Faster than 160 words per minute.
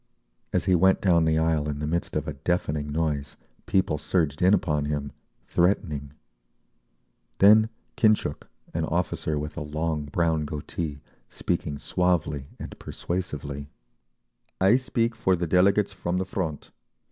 No: average, 140 wpm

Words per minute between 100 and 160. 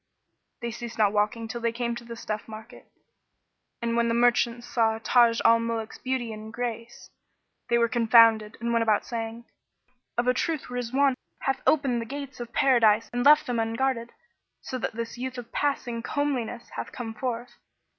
No: average, 175 wpm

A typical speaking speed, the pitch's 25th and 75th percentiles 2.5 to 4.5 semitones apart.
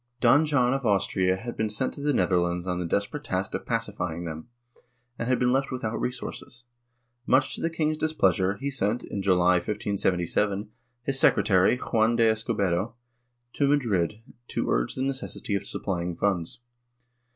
No: average, 165 wpm; wide, 5.6 semitones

